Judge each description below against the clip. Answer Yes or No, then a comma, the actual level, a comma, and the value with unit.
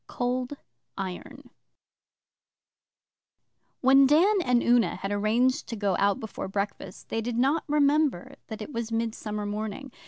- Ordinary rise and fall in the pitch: Yes, average, 4.5 semitones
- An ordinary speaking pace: No, slow, 130 wpm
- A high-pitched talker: Yes, high, 230 Hz